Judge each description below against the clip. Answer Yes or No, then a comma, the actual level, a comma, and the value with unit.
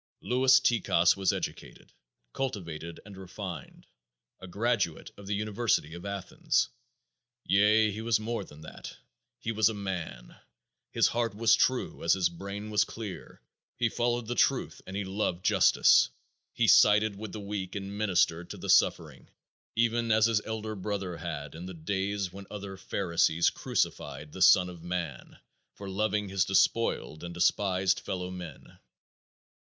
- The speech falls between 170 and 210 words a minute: No, average, 155 wpm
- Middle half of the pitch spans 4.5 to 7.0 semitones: No, average, 3.2 semitones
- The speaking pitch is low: Yes, low, 100 Hz